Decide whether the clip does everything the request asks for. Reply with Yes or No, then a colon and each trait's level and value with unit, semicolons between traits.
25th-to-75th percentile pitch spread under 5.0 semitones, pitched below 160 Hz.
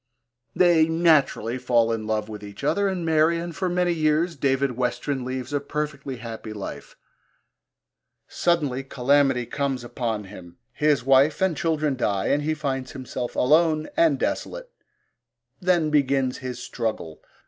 Yes: average, 4.4 semitones; medium, 140 Hz